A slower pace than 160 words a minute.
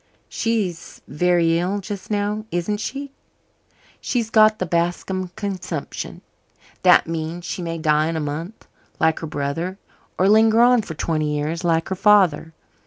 Yes: average, 150 wpm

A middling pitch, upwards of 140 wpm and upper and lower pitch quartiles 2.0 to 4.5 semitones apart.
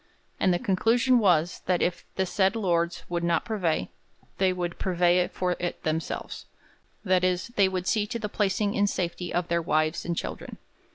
Yes: medium, 180 Hz; average, 180 wpm; narrow, 2.5 semitones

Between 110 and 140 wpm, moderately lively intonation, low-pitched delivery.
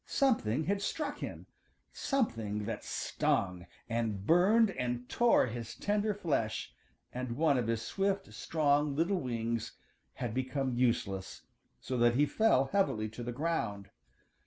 No: slow, 135 wpm; wide, 7.9 semitones; low, 130 Hz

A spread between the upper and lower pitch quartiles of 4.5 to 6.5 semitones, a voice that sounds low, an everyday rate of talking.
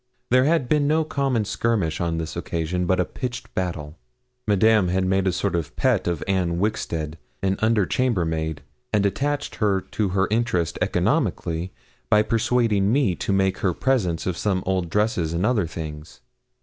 Yes: average, 4.9 semitones; very low, 95 Hz; average, 170 wpm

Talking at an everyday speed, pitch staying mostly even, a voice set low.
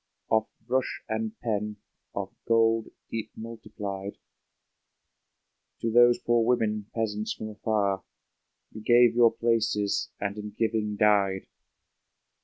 No: slow, 110 wpm; narrow, 1.6 semitones; low, 110 Hz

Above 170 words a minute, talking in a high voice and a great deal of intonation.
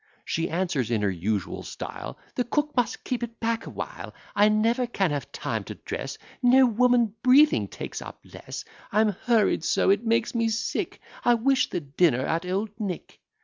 Yes: average, 185 wpm; high, 220 Hz; wide, 6.0 semitones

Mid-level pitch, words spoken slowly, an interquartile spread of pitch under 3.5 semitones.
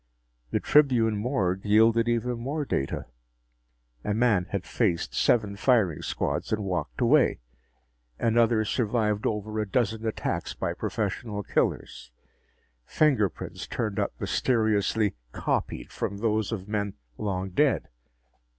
No: low, 110 Hz; slow, 120 wpm; narrow, 2.6 semitones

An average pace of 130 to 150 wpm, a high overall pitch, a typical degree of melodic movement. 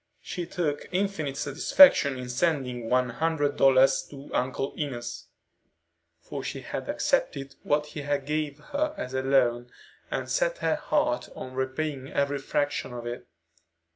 No: average, 140 wpm; medium, 140 Hz; average, 3.1 semitones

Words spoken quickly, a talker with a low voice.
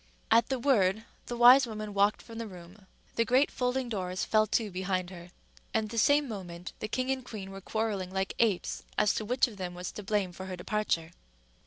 No: fast, 210 wpm; high, 210 Hz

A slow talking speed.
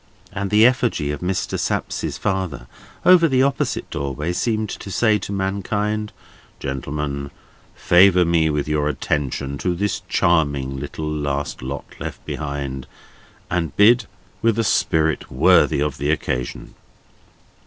Yes: slow, 130 wpm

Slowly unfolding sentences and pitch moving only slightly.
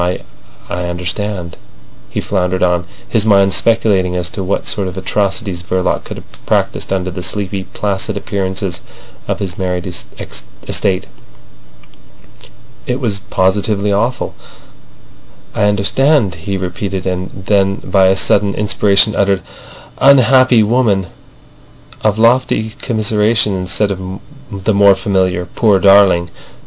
Yes: slow, 120 wpm; narrow, 2.2 semitones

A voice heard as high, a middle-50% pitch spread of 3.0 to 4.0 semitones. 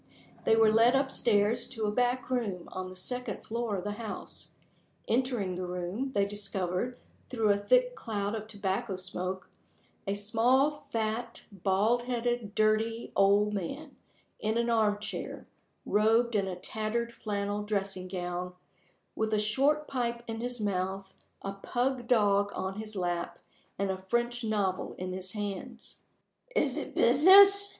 Yes: high, 215 Hz; average, 3.5 semitones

